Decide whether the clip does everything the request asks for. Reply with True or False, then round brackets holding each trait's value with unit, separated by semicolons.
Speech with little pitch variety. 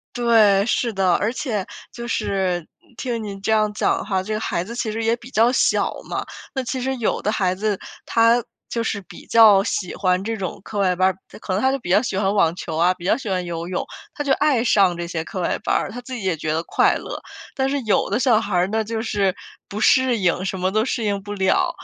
False (3.8 semitones)